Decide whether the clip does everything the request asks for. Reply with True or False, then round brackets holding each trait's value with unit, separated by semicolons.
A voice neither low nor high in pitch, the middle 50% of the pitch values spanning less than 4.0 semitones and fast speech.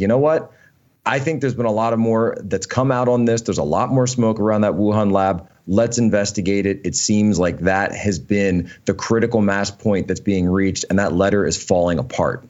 False (105 Hz; 2.9 semitones; 225 wpm)